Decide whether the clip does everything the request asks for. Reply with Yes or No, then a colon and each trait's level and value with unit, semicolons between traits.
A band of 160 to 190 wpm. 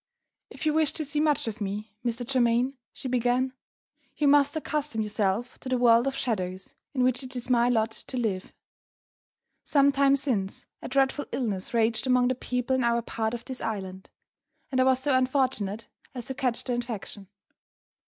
Yes: average, 180 wpm